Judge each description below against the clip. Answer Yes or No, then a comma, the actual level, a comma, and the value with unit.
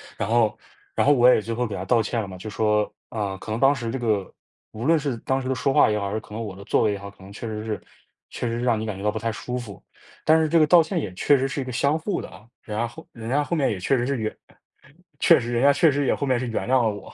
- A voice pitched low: Yes, low, 115 Hz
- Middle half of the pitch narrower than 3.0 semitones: No, average, 4.0 semitones